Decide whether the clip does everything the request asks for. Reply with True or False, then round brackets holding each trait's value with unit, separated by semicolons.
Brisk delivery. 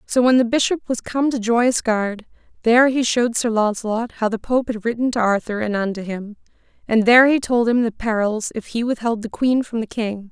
True (225 wpm)